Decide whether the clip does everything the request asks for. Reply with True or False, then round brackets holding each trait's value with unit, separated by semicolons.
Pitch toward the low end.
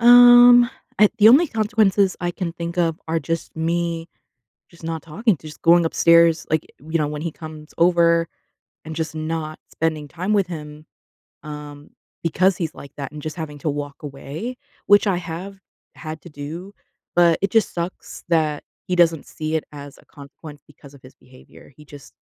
False (165 Hz)